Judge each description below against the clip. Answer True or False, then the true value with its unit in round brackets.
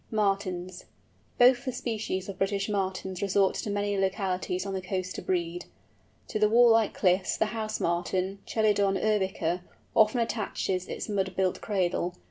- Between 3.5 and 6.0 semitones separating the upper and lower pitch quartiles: False (2.4 semitones)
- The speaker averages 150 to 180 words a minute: True (155 wpm)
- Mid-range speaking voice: False (195 Hz)